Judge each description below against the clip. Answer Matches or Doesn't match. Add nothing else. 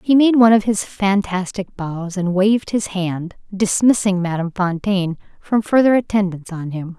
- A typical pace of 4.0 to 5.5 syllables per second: Matches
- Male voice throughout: Doesn't match